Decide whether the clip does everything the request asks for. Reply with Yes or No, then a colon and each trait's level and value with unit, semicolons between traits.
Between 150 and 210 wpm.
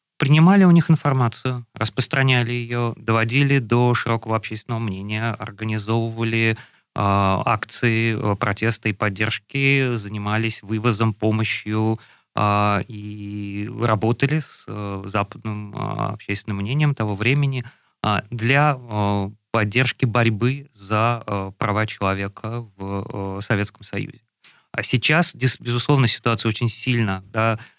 No: slow, 110 wpm